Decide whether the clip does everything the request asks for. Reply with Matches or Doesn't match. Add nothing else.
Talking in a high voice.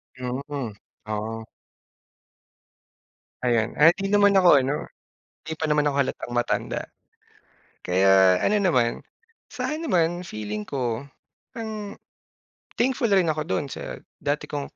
Doesn't match